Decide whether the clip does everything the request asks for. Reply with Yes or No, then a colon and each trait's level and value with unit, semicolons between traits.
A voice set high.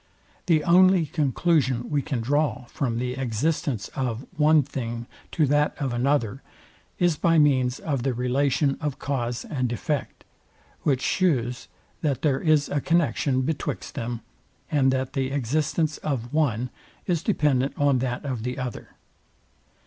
No: low, 135 Hz